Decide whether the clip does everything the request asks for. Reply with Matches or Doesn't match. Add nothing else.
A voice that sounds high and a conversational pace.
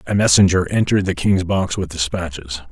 Doesn't match